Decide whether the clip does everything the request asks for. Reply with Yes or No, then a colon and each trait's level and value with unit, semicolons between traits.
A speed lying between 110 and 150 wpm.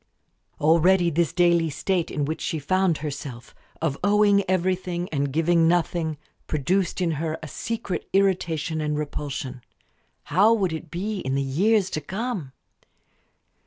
Yes: average, 140 wpm